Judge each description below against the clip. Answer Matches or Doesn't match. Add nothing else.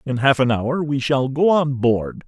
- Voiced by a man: Matches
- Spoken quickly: Matches